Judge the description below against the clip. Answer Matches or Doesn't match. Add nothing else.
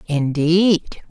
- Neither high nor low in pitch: Matches